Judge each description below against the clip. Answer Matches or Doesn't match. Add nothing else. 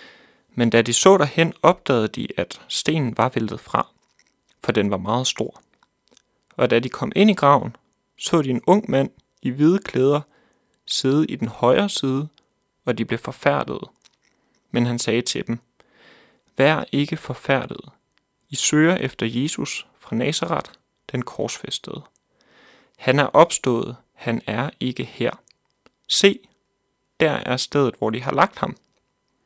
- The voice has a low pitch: Matches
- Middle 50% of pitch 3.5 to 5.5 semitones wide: Matches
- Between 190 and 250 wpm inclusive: Doesn't match